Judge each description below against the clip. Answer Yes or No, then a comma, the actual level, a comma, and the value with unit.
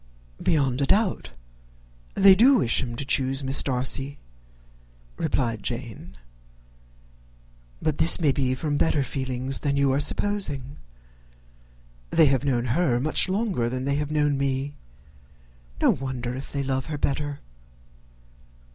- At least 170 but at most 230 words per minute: No, slow, 135 wpm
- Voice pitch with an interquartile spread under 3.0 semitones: Yes, narrow, 2.5 semitones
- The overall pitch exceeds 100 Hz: Yes, medium, 140 Hz